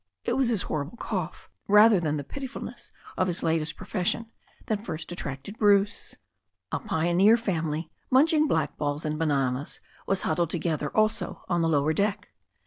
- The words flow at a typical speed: Yes, average, 155 wpm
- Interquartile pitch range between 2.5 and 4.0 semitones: No, wide, 5.5 semitones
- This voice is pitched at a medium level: Yes, medium, 175 Hz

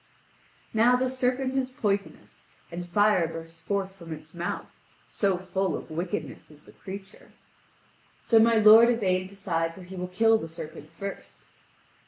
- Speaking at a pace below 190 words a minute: Yes, average, 155 wpm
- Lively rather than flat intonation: No, average, 4.6 semitones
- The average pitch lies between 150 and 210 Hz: Yes, high, 190 Hz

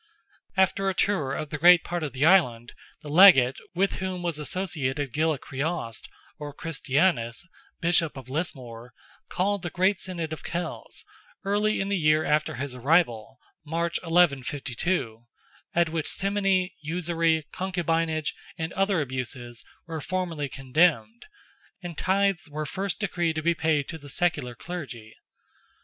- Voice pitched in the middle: Yes, medium, 160 Hz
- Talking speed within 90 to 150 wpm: Yes, average, 140 wpm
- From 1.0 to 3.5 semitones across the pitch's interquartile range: No, average, 4.4 semitones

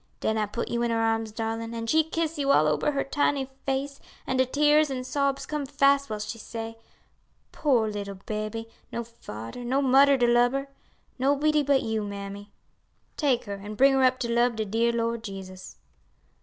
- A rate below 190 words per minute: No, average, 195 wpm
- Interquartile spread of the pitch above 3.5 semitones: Yes, average, 4.1 semitones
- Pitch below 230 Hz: No, high, 235 Hz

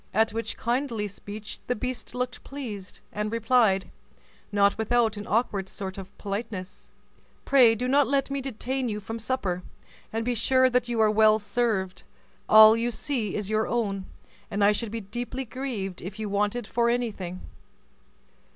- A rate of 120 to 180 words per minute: Yes, average, 165 wpm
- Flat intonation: No, average, 3.1 semitones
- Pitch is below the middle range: No, high, 220 Hz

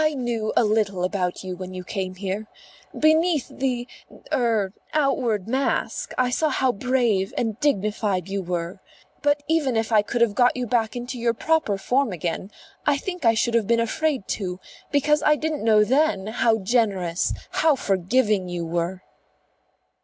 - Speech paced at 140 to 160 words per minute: No, average, 170 wpm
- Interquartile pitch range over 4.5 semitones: Yes, average, 5.3 semitones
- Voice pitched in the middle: No, high, 225 Hz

